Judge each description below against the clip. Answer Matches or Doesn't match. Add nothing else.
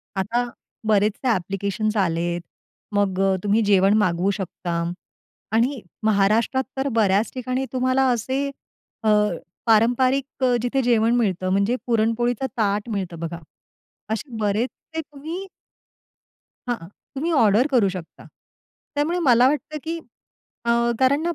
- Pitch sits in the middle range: Doesn't match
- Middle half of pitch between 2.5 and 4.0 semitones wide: Doesn't match